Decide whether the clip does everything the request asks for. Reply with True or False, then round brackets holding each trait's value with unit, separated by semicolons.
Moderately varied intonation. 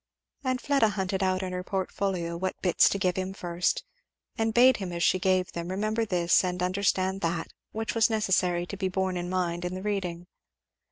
False (2.0 semitones)